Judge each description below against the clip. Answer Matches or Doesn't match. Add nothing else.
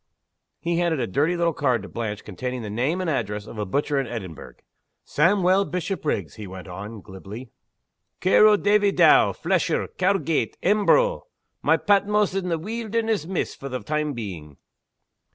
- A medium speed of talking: Matches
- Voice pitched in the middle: Matches